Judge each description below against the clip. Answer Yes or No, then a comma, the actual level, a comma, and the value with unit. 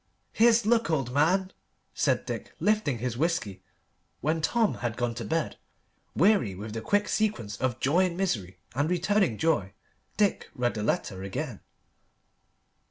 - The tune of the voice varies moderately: No, wide, 9.0 semitones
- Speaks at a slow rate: No, average, 150 wpm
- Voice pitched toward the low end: No, medium, 150 Hz